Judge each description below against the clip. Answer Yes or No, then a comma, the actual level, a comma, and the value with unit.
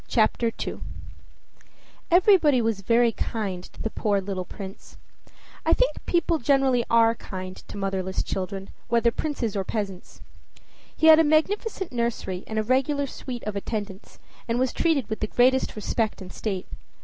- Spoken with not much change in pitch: No, average, 5.3 semitones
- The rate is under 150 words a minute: No, average, 155 wpm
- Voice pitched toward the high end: Yes, high, 230 Hz